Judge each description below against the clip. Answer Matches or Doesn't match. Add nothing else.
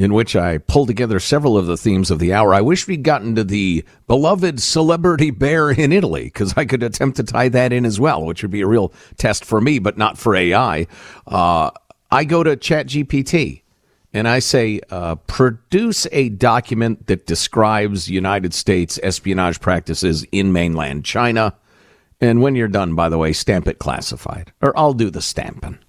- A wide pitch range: Matches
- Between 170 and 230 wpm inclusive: Matches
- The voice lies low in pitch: Matches